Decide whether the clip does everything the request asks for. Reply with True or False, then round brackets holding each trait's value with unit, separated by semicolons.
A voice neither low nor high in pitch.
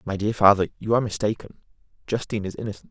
False (105 Hz)